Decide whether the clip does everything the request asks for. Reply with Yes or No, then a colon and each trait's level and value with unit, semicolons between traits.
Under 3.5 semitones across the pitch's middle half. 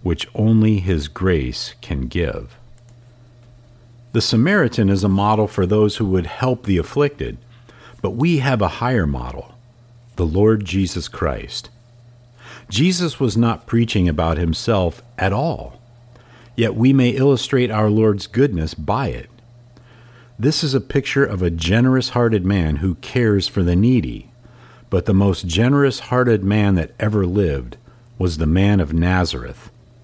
No: average, 4.3 semitones